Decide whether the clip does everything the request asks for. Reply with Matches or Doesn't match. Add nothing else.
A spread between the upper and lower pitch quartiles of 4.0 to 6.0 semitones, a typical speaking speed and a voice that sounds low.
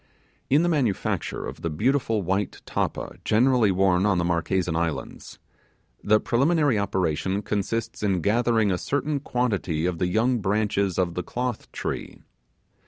Matches